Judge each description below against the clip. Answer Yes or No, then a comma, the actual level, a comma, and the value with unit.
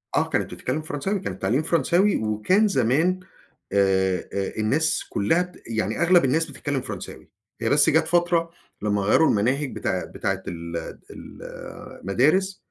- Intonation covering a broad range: Yes, wide, 8.7 semitones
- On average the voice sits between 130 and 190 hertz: Yes, medium, 140 Hz